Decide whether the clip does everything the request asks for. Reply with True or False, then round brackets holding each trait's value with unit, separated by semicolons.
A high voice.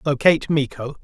False (145 Hz)